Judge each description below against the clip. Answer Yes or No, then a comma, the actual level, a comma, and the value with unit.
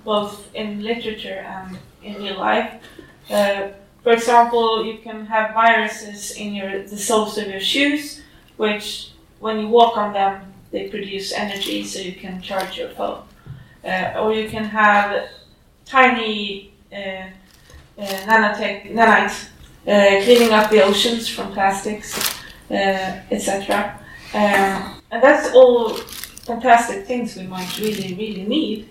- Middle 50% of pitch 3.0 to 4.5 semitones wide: No, narrow, 2.4 semitones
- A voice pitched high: Yes, high, 210 Hz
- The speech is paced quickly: No, average, 135 wpm